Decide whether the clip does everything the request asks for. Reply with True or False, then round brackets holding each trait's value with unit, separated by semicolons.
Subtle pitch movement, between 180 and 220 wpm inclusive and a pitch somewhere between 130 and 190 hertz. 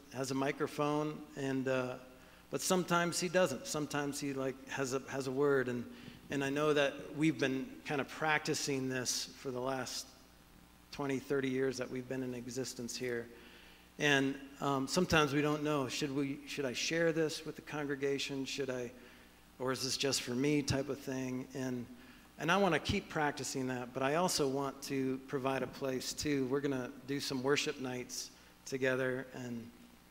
True (2.2 semitones; 185 wpm; 135 Hz)